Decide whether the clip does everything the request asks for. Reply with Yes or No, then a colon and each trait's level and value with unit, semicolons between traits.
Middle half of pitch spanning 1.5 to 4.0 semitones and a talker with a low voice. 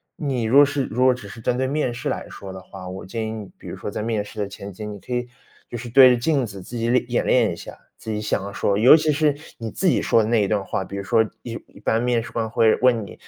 Yes: average, 3.6 semitones; low, 115 Hz